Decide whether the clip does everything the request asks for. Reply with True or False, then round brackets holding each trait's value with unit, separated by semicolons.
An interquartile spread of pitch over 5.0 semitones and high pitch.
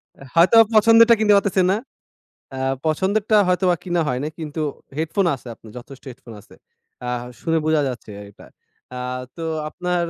False (5.5 semitones; 170 Hz)